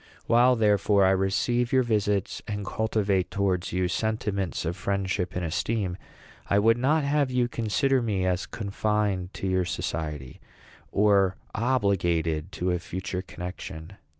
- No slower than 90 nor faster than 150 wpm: Yes, average, 140 wpm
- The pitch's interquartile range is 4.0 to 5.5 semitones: No, average, 3.3 semitones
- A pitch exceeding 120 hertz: No, low, 100 Hz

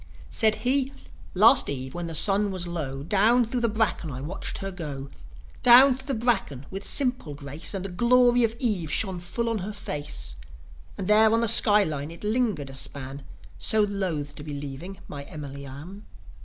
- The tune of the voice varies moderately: No, wide, 7.5 semitones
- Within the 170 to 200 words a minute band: Yes, average, 190 wpm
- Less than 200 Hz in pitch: Yes, high, 190 Hz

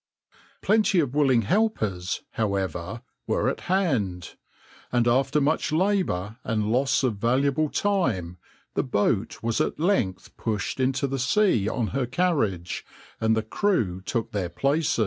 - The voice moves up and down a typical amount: No, wide, 6.7 semitones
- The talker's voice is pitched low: Yes, low, 120 Hz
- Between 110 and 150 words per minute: Yes, average, 140 wpm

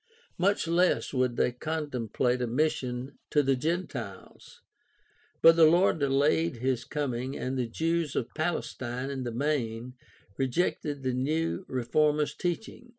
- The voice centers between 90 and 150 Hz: Yes, medium, 140 Hz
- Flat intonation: No, average, 4.4 semitones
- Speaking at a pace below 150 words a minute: Yes, slow, 135 wpm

